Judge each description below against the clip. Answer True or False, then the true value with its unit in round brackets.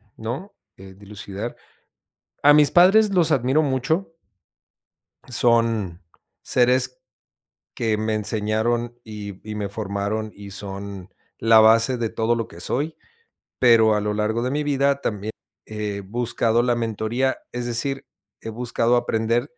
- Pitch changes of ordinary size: True (3.1 semitones)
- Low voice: True (115 Hz)